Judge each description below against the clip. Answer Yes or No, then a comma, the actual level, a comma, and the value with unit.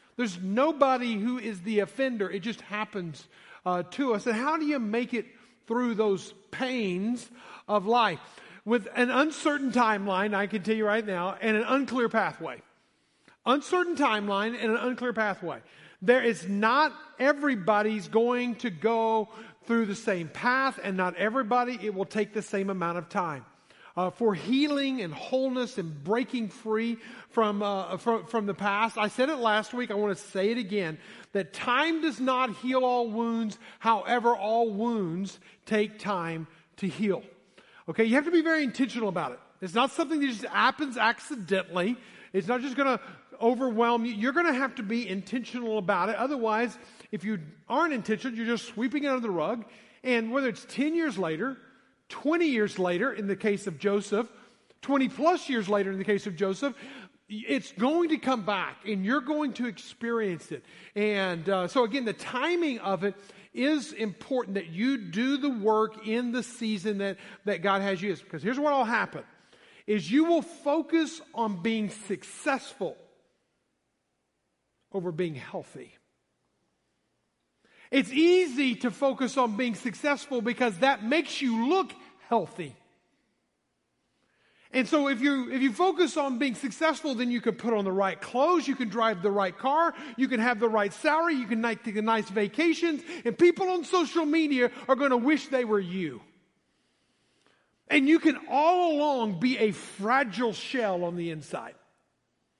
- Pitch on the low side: No, high, 235 Hz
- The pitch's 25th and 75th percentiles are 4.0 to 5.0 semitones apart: Yes, average, 4.5 semitones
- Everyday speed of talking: Yes, average, 170 wpm